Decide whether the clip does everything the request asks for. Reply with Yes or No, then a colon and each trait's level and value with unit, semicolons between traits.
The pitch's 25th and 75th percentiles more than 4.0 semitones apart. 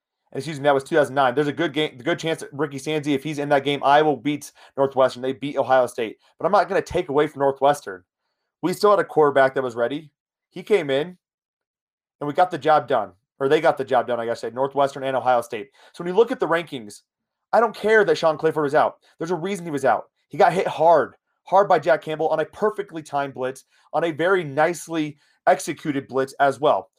No: average, 3.0 semitones